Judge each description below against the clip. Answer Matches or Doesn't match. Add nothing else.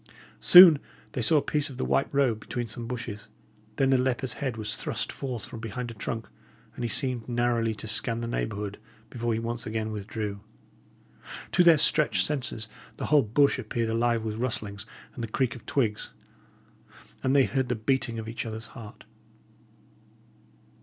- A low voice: Matches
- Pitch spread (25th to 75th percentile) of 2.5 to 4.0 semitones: Matches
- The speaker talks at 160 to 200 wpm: Matches